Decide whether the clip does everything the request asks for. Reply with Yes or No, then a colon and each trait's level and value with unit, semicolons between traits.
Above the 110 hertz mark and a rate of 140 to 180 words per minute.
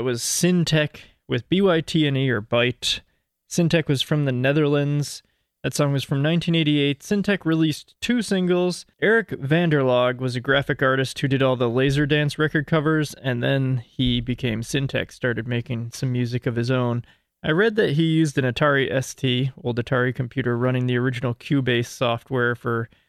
Yes: low, 135 Hz; average, 165 wpm